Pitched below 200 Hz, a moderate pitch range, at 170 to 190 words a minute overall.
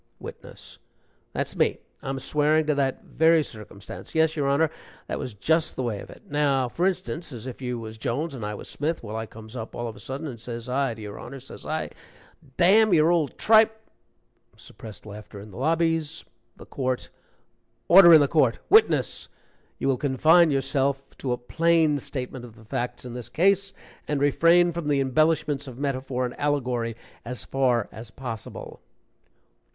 Yes: low, 135 Hz; average, 4.6 semitones; average, 185 wpm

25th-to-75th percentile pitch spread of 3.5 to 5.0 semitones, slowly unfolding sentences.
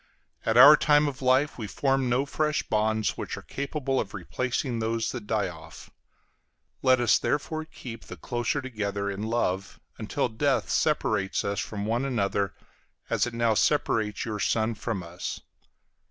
No: average, 4.4 semitones; average, 160 wpm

